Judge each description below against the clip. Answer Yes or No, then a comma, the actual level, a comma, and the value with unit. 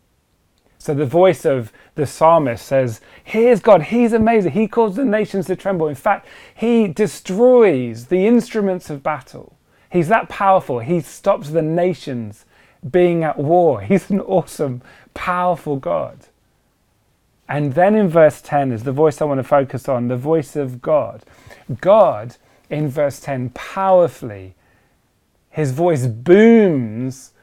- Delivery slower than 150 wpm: Yes, average, 140 wpm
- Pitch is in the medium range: Yes, medium, 160 Hz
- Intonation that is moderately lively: No, wide, 5.9 semitones